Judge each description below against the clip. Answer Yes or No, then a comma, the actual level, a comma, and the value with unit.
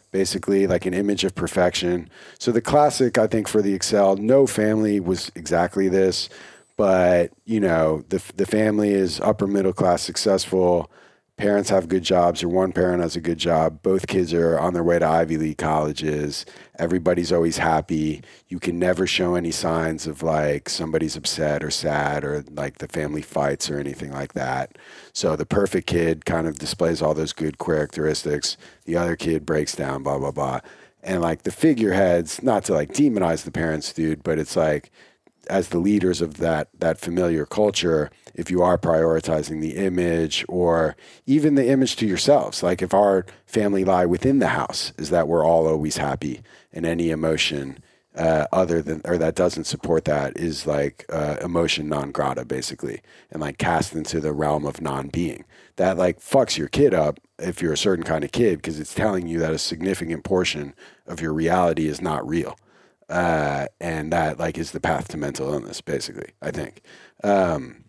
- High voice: No, very low, 85 Hz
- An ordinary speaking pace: Yes, average, 185 wpm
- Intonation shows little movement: No, average, 3.0 semitones